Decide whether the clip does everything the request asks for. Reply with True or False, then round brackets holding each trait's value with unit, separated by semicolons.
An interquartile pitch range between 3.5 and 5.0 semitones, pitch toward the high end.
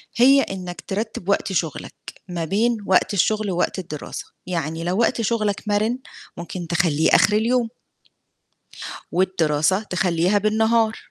True (4.2 semitones; 195 Hz)